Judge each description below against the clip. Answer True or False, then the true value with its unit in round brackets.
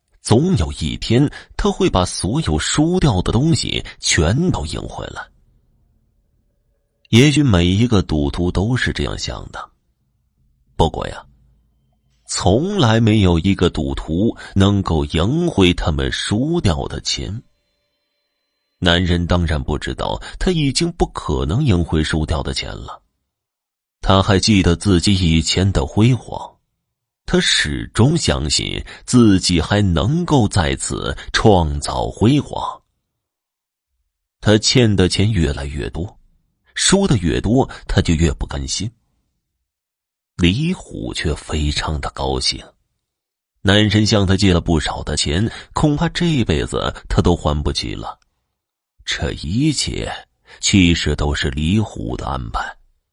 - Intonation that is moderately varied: False (6.7 semitones)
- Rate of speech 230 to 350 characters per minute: False (180 characters per minute)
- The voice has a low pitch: True (90 Hz)